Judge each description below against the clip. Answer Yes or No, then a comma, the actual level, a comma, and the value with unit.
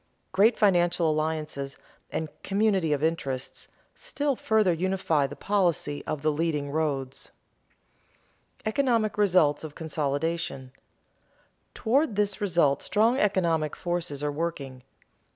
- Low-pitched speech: No, medium, 165 Hz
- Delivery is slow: Yes, slow, 115 wpm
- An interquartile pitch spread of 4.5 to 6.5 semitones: Yes, average, 5.3 semitones